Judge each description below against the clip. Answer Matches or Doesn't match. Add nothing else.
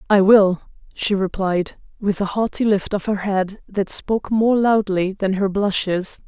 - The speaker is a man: Doesn't match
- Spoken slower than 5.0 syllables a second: Matches